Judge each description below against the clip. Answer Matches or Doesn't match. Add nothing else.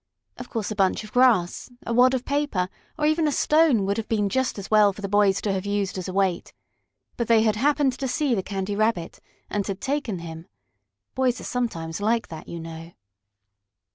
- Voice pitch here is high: Matches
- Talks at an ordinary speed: Doesn't match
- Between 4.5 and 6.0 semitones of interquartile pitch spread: Matches